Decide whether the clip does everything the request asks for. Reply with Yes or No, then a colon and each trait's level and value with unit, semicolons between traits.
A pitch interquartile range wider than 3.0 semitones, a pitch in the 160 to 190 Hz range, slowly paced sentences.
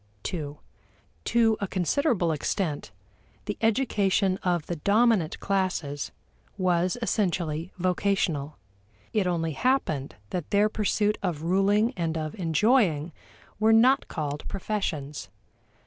Yes: average, 4.7 semitones; medium, 185 Hz; slow, 110 wpm